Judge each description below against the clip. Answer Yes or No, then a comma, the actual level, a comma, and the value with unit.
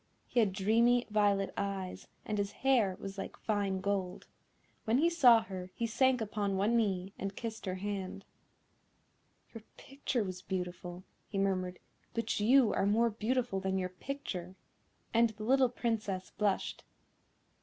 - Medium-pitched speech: No, high, 205 Hz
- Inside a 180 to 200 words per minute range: No, average, 150 wpm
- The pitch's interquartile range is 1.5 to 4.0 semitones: Yes, average, 3.4 semitones